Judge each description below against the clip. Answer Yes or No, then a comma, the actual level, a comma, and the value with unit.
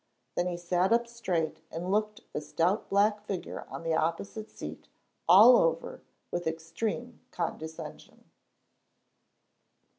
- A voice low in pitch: No, medium, 180 Hz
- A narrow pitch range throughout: No, average, 4.4 semitones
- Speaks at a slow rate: Yes, slow, 120 wpm